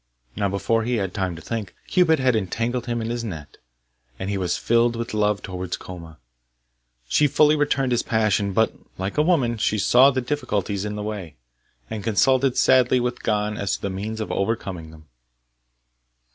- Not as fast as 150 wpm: No, average, 185 wpm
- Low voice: Yes, low, 110 Hz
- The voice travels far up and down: No, average, 3.9 semitones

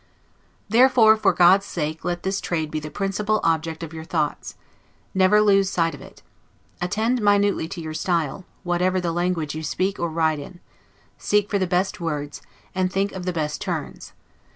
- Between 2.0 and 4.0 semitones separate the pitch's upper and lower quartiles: Yes, average, 3.5 semitones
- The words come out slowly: No, average, 175 wpm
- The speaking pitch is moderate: Yes, medium, 180 Hz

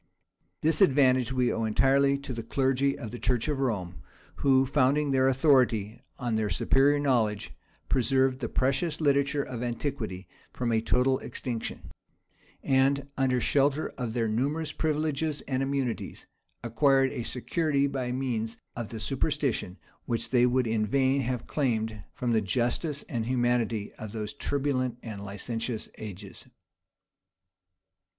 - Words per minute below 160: Yes, average, 140 wpm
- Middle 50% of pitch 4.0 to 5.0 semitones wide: No, average, 3.3 semitones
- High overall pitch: No, low, 130 Hz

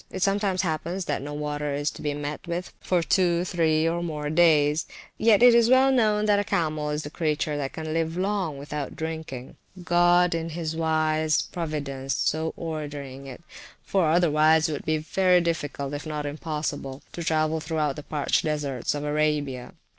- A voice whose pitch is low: No, medium, 155 Hz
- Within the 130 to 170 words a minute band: No, average, 185 wpm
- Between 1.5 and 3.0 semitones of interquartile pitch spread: Yes, average, 2.7 semitones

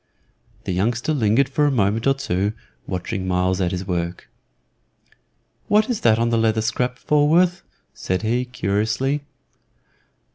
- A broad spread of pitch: Yes, wide, 6.0 semitones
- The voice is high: No, low, 115 Hz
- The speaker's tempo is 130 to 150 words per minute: Yes, average, 140 wpm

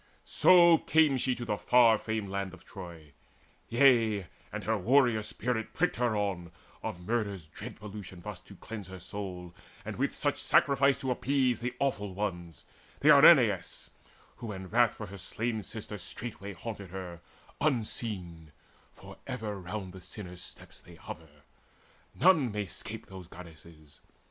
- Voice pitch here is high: No, low, 105 Hz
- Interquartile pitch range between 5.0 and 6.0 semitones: No, average, 4.6 semitones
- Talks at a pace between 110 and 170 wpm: Yes, average, 155 wpm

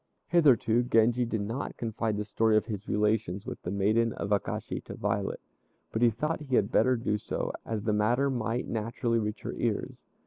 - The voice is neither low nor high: No, low, 110 Hz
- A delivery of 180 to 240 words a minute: Yes, average, 195 wpm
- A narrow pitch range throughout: Yes, narrow, 2.3 semitones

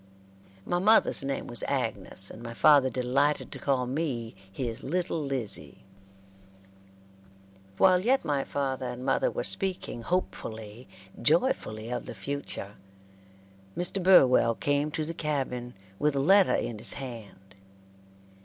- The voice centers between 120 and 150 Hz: Yes, low, 135 Hz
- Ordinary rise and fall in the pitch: Yes, average, 4.8 semitones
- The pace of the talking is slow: Yes, slow, 130 wpm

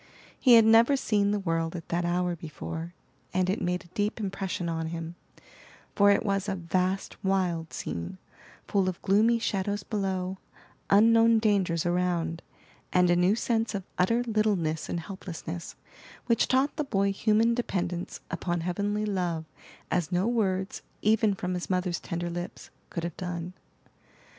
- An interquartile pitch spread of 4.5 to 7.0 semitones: No, average, 3.2 semitones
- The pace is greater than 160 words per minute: No, average, 155 wpm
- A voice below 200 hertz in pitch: Yes, medium, 185 Hz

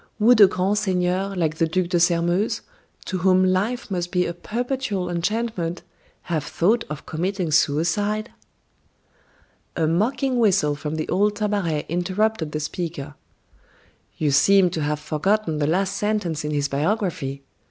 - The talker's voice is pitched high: No, medium, 180 Hz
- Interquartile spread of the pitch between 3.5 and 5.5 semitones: Yes, average, 4.6 semitones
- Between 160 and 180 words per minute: No, average, 150 wpm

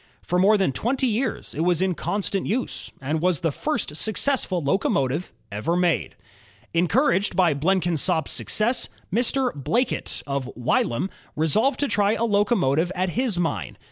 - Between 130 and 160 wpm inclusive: Yes, average, 145 wpm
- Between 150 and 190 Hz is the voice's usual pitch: Yes, medium, 185 Hz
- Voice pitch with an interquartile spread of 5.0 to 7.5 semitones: Yes, wide, 5.6 semitones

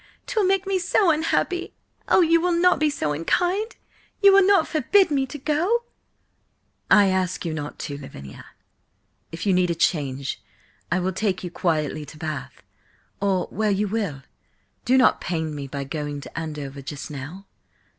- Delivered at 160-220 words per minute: Yes, average, 170 wpm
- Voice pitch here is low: No, high, 190 Hz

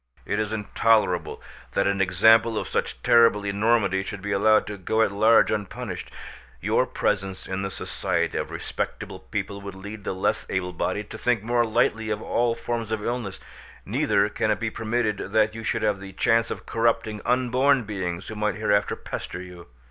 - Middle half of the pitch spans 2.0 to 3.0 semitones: Yes, narrow, 2.5 semitones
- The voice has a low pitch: Yes, low, 105 Hz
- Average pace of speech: Yes, average, 185 wpm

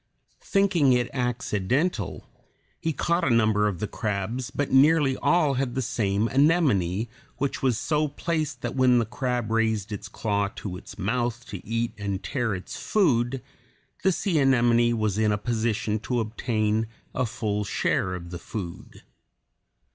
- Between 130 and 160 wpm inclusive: Yes, average, 155 wpm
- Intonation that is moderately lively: Yes, average, 4.2 semitones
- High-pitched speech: No, low, 120 Hz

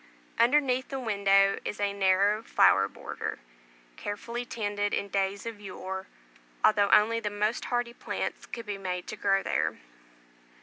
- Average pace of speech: Yes, average, 145 wpm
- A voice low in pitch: No, high, 205 Hz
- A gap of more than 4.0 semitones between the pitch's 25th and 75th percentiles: No, narrow, 2.6 semitones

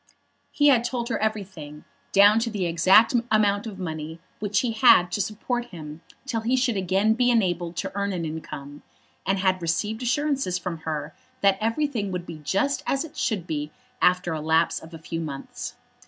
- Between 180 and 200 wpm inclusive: Yes, average, 185 wpm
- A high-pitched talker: Yes, high, 195 Hz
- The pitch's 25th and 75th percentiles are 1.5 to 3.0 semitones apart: No, wide, 5.4 semitones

